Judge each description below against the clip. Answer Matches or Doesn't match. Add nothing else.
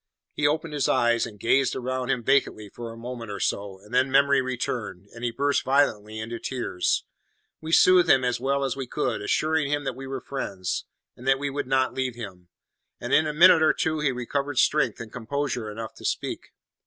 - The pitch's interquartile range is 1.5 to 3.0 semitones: Doesn't match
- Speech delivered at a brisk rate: Matches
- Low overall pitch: Matches